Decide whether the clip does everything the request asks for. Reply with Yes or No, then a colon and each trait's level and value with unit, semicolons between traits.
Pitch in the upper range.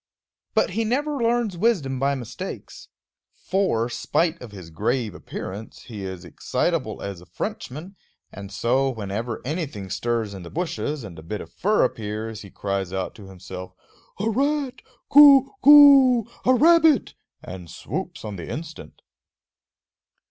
No: low, 125 Hz